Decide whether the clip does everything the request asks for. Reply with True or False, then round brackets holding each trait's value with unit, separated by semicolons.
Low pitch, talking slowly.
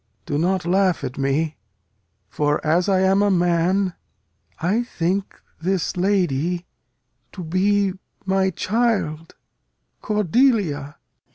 False (185 Hz; 105 wpm)